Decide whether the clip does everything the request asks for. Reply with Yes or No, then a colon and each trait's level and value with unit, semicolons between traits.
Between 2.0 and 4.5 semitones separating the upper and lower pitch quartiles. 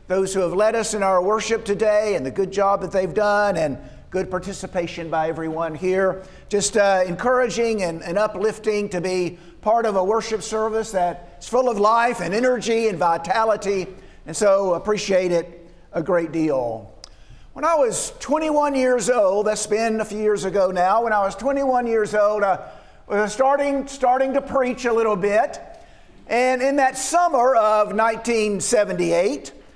Yes: average, 3.8 semitones